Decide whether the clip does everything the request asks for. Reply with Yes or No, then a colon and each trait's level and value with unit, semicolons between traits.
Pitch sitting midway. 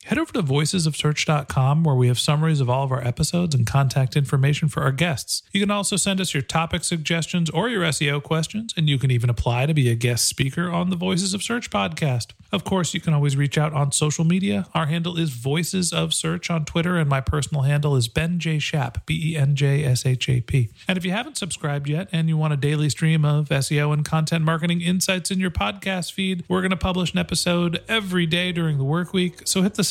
Yes: medium, 160 Hz